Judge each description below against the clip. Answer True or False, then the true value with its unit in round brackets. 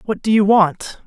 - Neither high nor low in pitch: False (205 Hz)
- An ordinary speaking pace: False (225 wpm)